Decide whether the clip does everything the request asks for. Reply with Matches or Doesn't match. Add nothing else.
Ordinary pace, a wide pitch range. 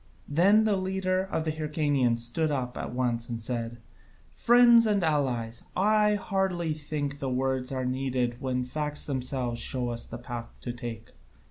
Matches